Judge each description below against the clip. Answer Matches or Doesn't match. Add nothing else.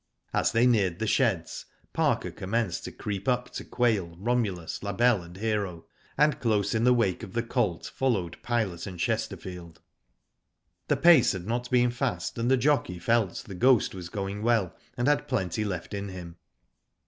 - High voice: Doesn't match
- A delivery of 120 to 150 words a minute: Doesn't match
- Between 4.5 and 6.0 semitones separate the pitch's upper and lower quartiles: Matches